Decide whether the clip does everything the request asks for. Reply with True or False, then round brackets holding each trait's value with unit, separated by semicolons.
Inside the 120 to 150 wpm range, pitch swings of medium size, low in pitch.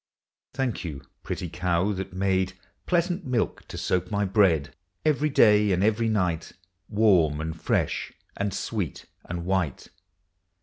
True (135 wpm; 3.9 semitones; 95 Hz)